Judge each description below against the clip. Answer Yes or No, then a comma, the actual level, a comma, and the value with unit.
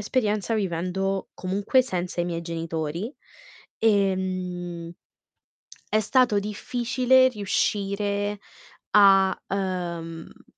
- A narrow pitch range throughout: No, average, 3.0 semitones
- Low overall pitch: No, high, 195 Hz